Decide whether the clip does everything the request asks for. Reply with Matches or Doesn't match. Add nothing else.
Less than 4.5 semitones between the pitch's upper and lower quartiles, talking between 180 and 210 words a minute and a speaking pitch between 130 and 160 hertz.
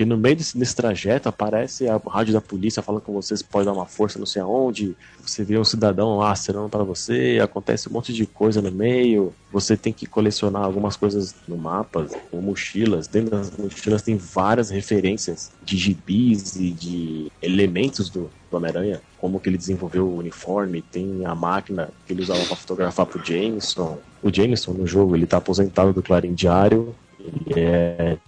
Doesn't match